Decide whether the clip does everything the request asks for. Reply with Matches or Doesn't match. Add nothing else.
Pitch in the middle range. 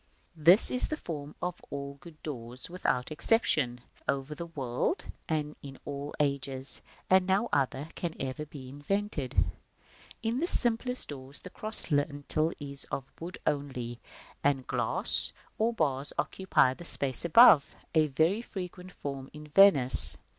Matches